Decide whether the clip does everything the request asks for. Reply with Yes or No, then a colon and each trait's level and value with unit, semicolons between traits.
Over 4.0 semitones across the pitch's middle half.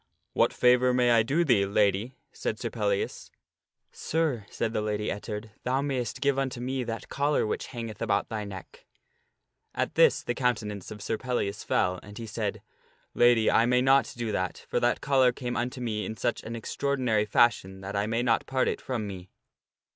No: average, 3.4 semitones